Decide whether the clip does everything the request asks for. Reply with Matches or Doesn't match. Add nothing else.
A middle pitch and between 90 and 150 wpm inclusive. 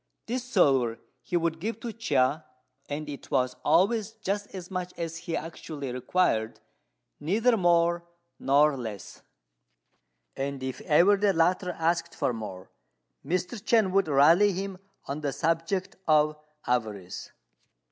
Matches